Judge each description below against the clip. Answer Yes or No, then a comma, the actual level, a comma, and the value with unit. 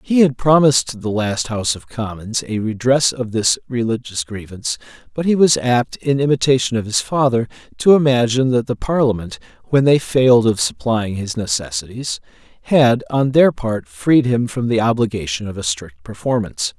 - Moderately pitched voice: No, low, 120 Hz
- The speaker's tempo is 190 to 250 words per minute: No, average, 175 wpm